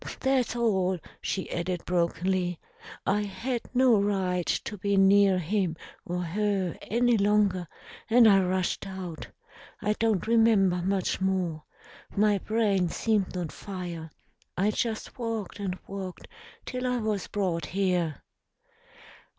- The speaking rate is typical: No, slow, 125 wpm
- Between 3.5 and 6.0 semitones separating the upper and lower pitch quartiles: No, average, 2.9 semitones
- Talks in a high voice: Yes, high, 195 Hz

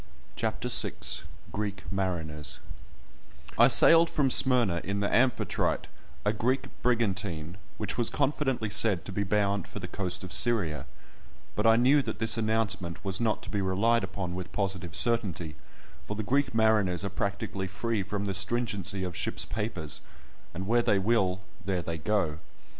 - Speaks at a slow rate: No, average, 160 wpm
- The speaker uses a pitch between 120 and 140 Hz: No, low, 100 Hz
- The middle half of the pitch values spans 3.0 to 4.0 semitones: Yes, average, 3.4 semitones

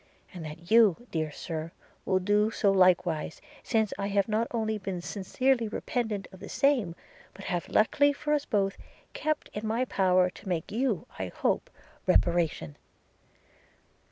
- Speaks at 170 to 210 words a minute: No, average, 160 wpm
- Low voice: No, high, 200 Hz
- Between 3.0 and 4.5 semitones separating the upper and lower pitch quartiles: Yes, average, 4.2 semitones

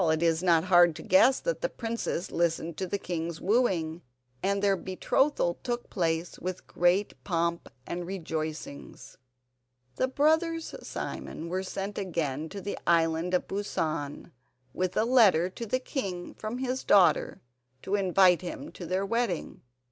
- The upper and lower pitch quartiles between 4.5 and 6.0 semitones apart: No, average, 3.4 semitones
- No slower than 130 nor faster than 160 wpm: Yes, average, 150 wpm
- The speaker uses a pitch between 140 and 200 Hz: Yes, medium, 185 Hz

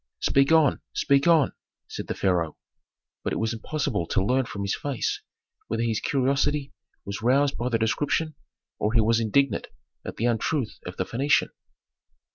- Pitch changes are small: No, average, 4.3 semitones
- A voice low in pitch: Yes, low, 120 Hz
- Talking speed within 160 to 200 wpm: Yes, average, 165 wpm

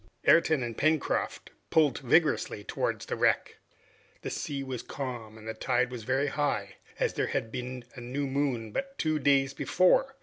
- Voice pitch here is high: No, low, 135 Hz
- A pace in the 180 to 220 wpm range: No, average, 165 wpm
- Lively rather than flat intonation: No, average, 3.5 semitones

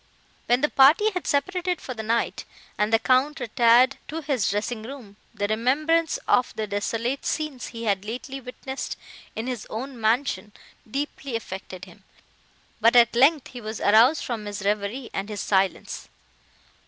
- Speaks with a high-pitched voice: Yes, high, 240 Hz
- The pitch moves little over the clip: No, average, 4.1 semitones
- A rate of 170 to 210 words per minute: No, average, 160 wpm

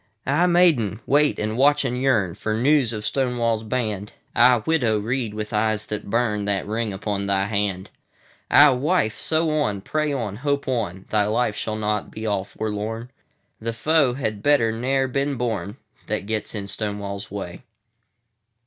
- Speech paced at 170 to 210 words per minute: No, average, 140 wpm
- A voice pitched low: Yes, low, 110 Hz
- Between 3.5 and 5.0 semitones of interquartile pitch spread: Yes, average, 4.2 semitones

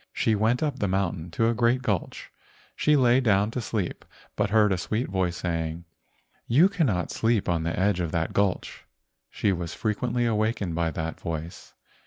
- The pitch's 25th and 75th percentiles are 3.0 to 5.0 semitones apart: No, wide, 5.4 semitones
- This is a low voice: Yes, low, 100 Hz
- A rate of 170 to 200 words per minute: Yes, average, 180 wpm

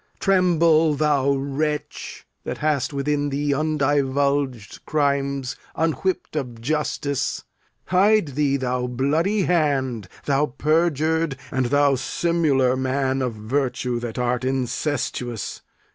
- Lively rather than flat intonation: No, average, 2.8 semitones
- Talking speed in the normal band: No, slow, 105 wpm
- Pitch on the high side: No, medium, 140 Hz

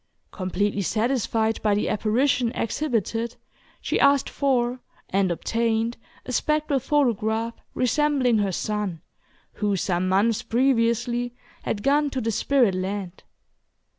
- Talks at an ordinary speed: No, slow, 115 wpm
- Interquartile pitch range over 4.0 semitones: No, average, 3.7 semitones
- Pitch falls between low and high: No, high, 230 Hz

